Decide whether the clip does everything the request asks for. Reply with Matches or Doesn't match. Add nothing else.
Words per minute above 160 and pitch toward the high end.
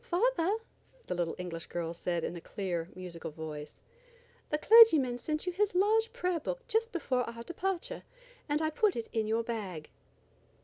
Matches